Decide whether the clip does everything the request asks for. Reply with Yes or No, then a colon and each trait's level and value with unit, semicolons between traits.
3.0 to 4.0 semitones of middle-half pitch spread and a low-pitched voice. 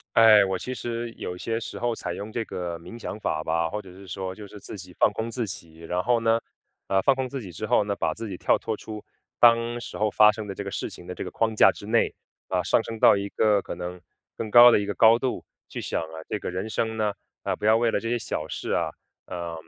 Yes: average, 3.7 semitones; low, 105 Hz